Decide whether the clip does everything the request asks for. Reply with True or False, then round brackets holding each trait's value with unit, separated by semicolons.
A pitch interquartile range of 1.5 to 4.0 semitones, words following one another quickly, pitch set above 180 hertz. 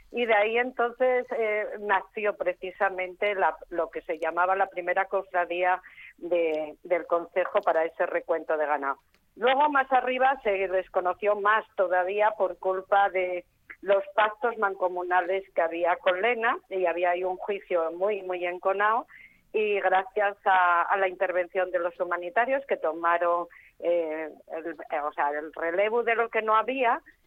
False (3.2 semitones; 150 wpm; 190 Hz)